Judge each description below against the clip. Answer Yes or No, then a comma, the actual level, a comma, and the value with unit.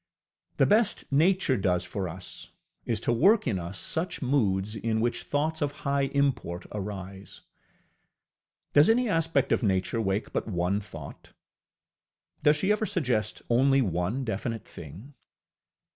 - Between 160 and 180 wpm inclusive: No, average, 140 wpm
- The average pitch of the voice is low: Yes, low, 115 Hz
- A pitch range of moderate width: No, wide, 7.1 semitones